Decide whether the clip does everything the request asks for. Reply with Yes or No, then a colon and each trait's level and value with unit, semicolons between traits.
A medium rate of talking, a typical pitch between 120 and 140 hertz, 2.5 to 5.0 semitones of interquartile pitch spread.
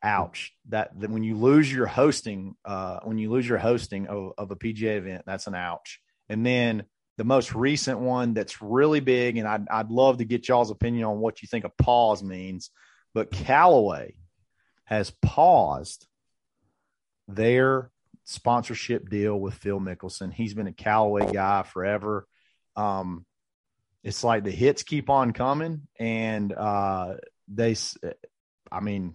No: average, 155 wpm; low, 110 Hz; average, 3.4 semitones